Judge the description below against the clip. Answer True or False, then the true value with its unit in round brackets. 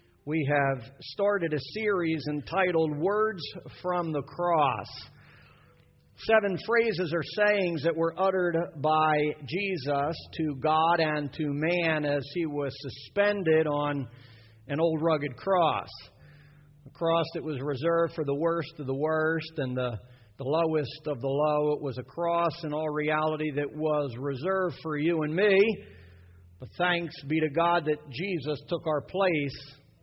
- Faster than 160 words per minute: False (150 wpm)